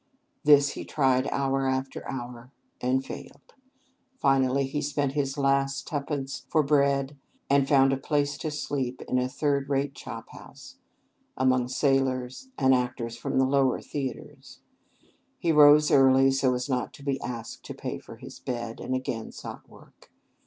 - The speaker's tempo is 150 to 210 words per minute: Yes, average, 160 wpm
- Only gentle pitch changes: Yes, narrow, 1.5 semitones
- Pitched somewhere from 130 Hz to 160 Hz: Yes, low, 135 Hz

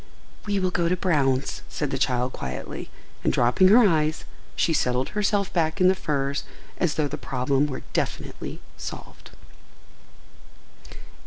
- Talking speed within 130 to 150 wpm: Yes, average, 145 wpm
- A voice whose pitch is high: No, medium, 150 Hz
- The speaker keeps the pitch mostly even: No, wide, 5.6 semitones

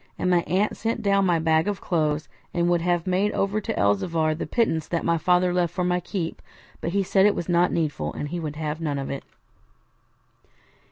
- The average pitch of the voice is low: No, medium, 175 Hz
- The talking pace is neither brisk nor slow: No, fast, 215 wpm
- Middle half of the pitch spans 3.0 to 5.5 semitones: No, narrow, 2.6 semitones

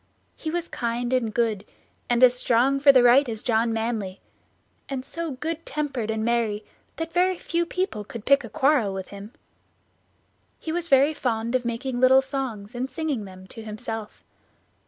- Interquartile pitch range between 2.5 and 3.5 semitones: No, average, 3.9 semitones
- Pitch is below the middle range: No, high, 245 Hz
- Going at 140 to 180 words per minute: Yes, average, 175 wpm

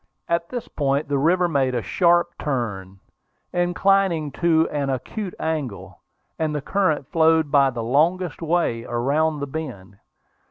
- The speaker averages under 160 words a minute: Yes, average, 145 wpm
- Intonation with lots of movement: No, average, 4.2 semitones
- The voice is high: No, medium, 150 Hz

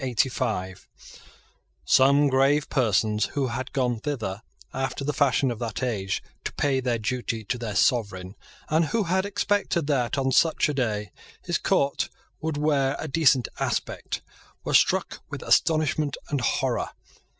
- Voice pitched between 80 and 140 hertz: Yes, low, 135 Hz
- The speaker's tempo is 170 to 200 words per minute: No, average, 145 wpm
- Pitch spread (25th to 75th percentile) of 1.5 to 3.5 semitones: No, average, 3.9 semitones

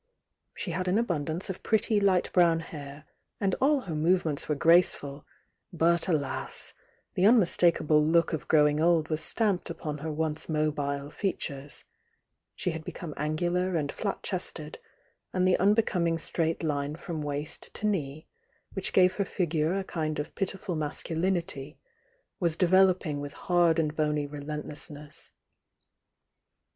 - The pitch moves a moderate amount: Yes, average, 3.4 semitones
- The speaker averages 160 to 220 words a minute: No, average, 140 wpm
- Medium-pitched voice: Yes, medium, 165 Hz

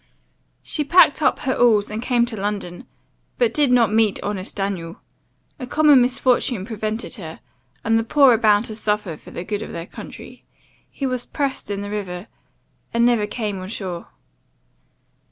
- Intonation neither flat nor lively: Yes, average, 3.7 semitones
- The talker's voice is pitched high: Yes, high, 220 Hz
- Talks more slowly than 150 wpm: No, average, 170 wpm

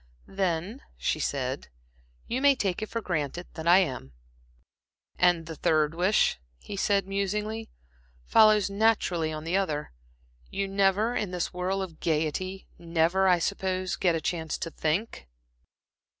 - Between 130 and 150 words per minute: Yes, average, 145 wpm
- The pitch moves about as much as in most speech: Yes, average, 3.6 semitones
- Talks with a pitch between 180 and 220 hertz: Yes, medium, 185 Hz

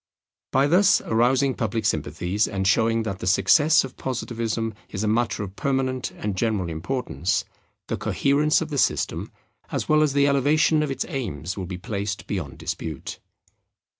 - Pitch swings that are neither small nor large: No, wide, 6.0 semitones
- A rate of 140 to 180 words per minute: Yes, average, 165 wpm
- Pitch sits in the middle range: No, low, 115 Hz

